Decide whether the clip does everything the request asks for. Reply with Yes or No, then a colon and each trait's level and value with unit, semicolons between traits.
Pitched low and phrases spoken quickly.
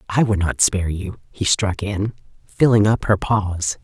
No: low, 100 Hz; average, 190 wpm